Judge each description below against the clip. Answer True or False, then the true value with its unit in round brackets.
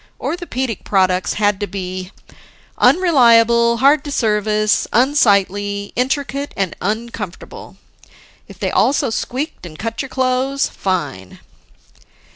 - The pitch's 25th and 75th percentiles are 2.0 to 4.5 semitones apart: False (4.9 semitones)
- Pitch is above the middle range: True (225 Hz)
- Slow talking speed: True (105 wpm)